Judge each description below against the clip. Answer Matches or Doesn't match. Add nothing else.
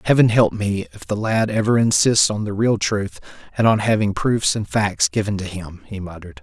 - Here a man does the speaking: Matches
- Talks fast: Matches